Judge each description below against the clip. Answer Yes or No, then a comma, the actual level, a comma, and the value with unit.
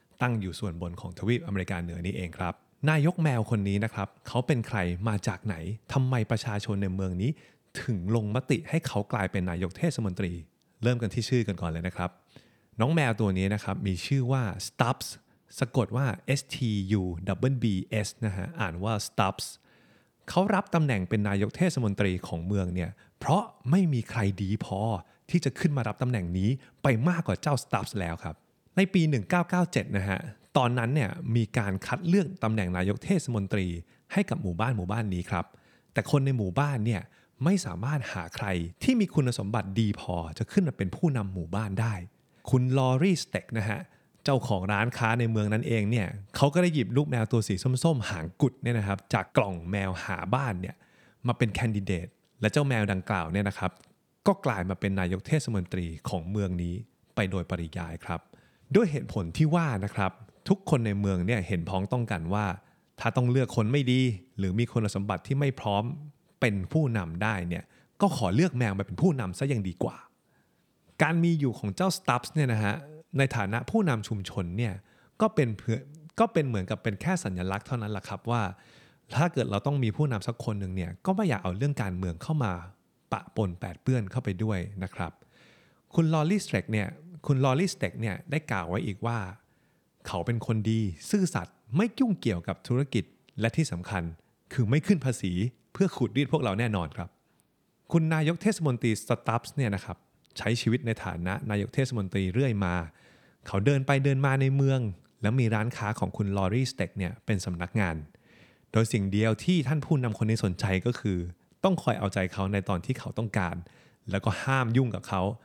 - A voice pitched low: Yes, low, 110 Hz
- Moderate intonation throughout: No, wide, 5.7 semitones